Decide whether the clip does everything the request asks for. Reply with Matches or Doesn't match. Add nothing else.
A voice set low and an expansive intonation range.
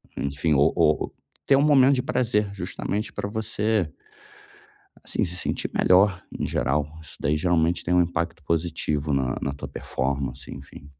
Matches